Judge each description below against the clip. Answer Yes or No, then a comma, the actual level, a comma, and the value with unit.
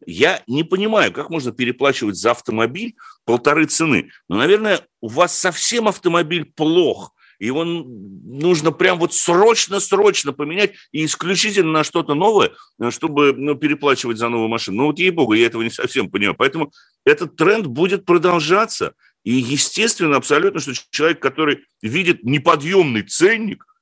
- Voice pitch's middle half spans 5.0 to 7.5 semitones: Yes, wide, 5.4 semitones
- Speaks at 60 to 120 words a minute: No, average, 145 wpm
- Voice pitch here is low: No, medium, 170 Hz